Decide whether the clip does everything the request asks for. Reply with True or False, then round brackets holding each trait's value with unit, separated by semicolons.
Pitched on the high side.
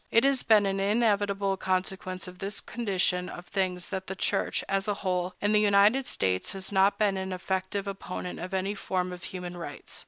True (195 Hz)